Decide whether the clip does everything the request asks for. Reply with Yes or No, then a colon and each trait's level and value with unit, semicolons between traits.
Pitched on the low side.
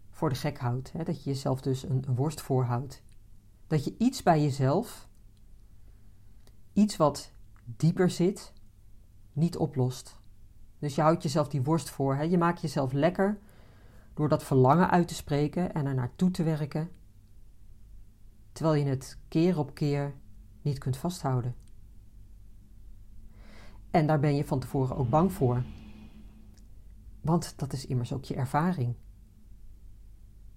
Yes: low, 130 Hz